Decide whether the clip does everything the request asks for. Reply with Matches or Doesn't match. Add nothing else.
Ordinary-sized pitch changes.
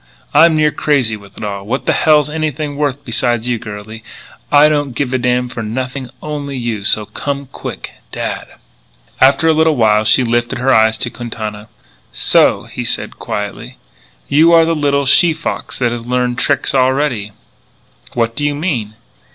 Matches